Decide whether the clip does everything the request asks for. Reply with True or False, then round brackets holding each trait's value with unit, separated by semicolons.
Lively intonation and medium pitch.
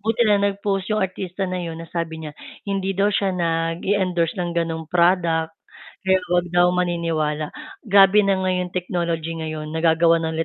False (2.7 semitones; 175 Hz)